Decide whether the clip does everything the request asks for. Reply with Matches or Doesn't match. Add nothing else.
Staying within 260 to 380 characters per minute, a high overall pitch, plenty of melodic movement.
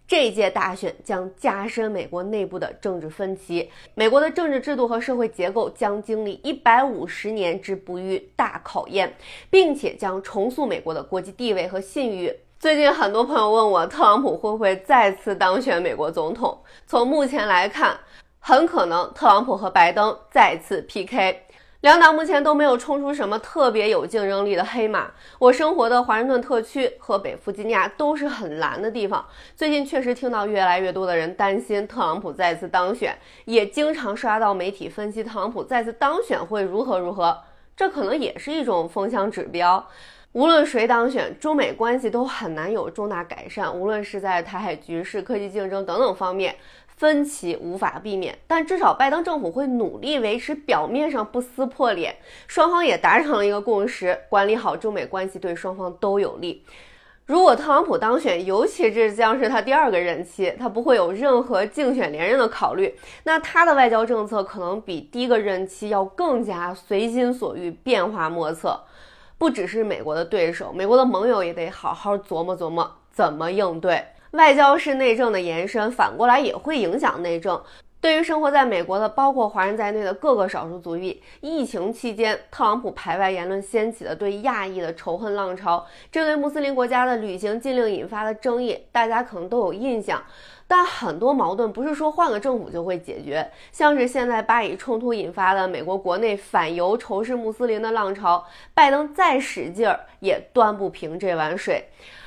Matches